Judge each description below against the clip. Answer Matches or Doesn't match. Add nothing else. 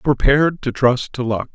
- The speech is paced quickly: Doesn't match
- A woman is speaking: Doesn't match